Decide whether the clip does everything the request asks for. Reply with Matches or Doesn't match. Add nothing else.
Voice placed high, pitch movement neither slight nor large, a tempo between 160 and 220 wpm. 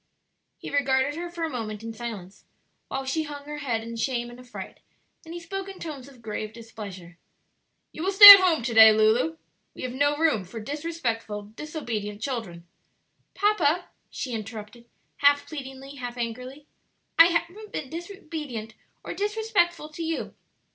Doesn't match